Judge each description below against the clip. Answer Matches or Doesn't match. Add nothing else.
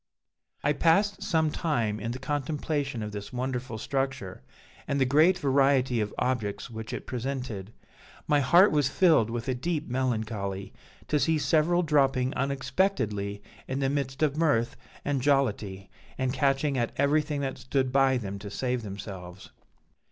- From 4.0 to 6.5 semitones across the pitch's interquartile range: Matches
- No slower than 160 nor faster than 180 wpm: Doesn't match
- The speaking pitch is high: Doesn't match